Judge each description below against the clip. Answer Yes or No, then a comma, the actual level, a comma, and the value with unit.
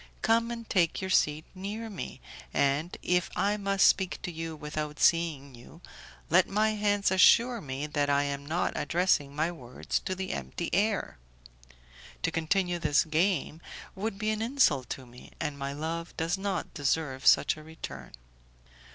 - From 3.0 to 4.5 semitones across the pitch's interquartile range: No, average, 5.0 semitones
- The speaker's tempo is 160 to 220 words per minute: Yes, average, 165 wpm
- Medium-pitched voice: Yes, medium, 170 Hz